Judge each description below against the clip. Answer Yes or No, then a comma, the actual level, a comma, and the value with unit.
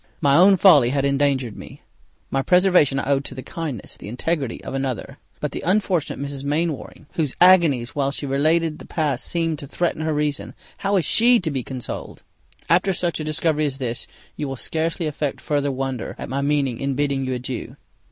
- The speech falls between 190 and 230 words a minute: Yes, average, 195 wpm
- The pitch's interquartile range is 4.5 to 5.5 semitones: No, average, 3.4 semitones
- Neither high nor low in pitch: Yes, medium, 145 Hz